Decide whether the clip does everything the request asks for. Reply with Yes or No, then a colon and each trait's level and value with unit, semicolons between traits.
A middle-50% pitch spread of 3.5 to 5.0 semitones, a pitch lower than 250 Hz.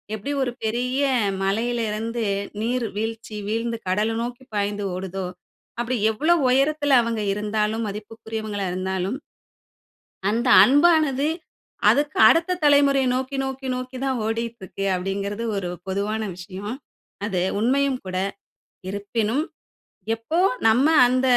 Yes: average, 4.1 semitones; high, 230 Hz